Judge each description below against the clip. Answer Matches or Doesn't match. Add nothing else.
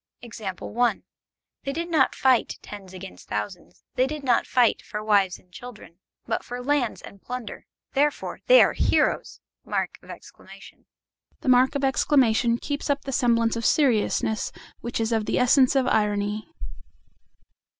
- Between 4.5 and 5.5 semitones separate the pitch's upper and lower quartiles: Doesn't match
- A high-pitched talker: Matches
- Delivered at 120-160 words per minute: Matches